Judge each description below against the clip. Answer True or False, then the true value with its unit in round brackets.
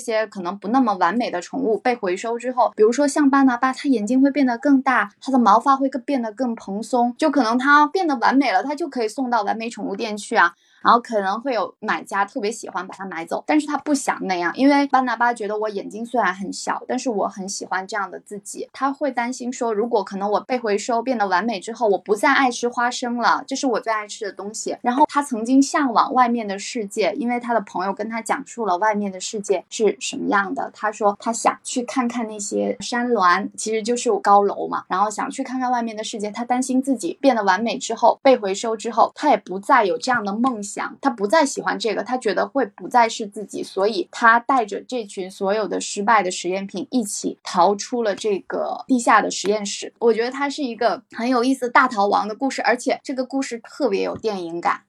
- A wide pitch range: False (4.3 semitones)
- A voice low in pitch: False (235 Hz)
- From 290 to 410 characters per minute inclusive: True (340 characters per minute)